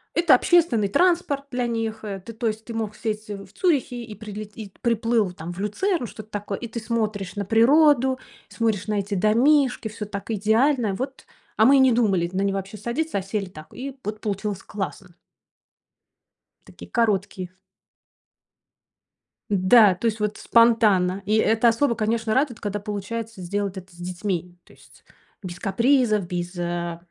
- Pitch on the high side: Yes, high, 215 Hz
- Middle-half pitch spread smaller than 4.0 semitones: Yes, average, 3.2 semitones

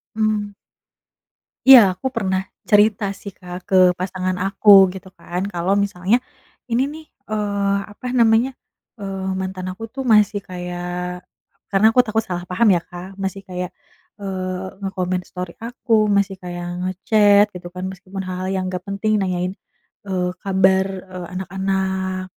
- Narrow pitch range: Yes, narrow, 1.9 semitones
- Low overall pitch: No, high, 190 Hz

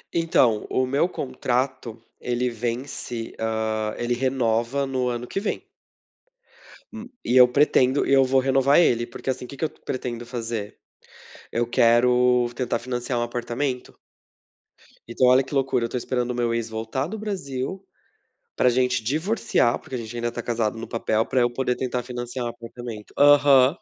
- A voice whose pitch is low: Yes, low, 125 Hz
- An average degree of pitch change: No, narrow, 2.1 semitones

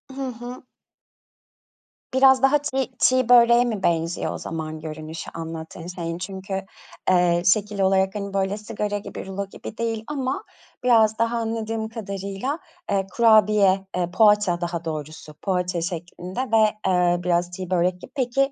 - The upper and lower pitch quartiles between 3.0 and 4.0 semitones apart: No, average, 4.5 semitones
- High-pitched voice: Yes, high, 195 Hz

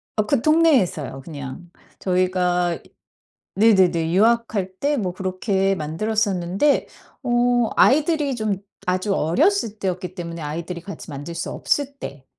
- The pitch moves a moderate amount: Yes, average, 5.0 semitones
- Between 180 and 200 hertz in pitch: Yes, high, 190 Hz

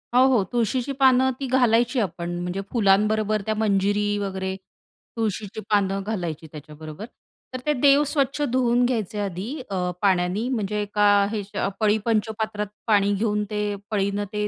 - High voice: Yes, high, 210 Hz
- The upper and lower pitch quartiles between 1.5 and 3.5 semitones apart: Yes, average, 3.1 semitones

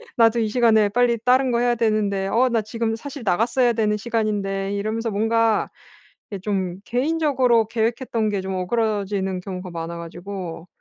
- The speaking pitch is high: Yes, high, 220 Hz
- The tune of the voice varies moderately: Yes, average, 3.2 semitones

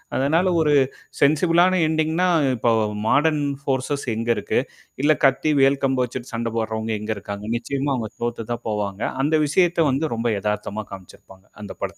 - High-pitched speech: No, low, 135 Hz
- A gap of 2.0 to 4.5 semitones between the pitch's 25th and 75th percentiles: No, wide, 5.4 semitones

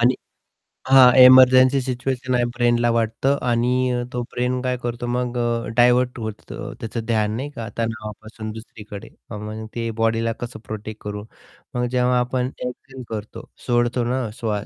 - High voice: No, low, 120 Hz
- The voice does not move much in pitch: Yes, narrow, 2.0 semitones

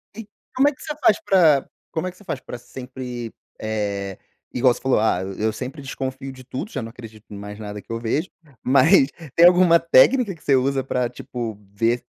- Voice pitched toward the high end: No, low, 130 Hz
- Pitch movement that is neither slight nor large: No, wide, 6.1 semitones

